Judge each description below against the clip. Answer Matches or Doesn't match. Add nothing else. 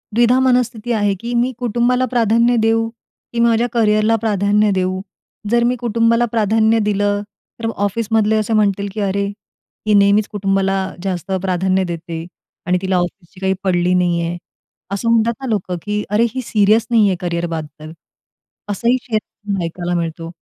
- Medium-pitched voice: Doesn't match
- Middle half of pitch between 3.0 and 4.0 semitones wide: Matches